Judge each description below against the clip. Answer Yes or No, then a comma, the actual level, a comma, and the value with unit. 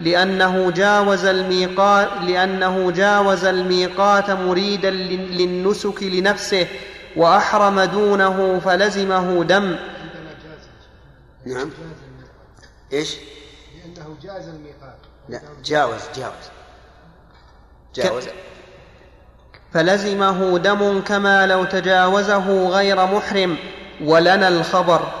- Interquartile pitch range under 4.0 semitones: Yes, narrow, 2.4 semitones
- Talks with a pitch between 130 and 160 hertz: No, medium, 185 Hz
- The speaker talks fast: No, average, 70 wpm